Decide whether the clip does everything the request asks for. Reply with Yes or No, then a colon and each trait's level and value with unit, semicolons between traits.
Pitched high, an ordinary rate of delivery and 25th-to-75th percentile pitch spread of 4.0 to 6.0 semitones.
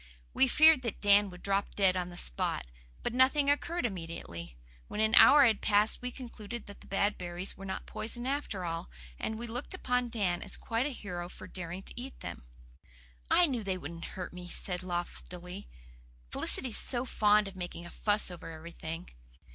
Yes: high, 200 Hz; average, 190 wpm; average, 5.2 semitones